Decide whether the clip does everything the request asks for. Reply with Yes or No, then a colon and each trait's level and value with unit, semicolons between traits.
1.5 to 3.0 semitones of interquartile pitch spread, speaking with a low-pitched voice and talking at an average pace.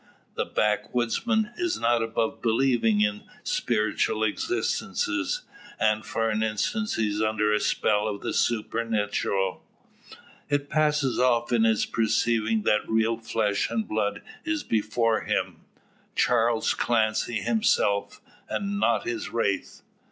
No: narrow, 2.6 semitones; low, 115 Hz; slow, 125 wpm